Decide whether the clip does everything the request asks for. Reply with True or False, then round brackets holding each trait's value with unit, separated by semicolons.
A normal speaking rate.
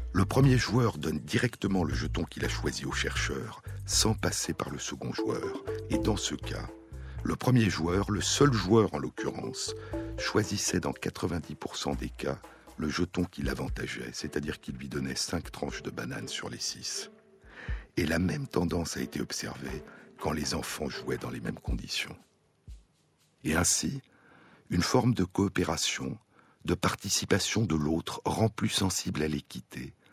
True (160 wpm)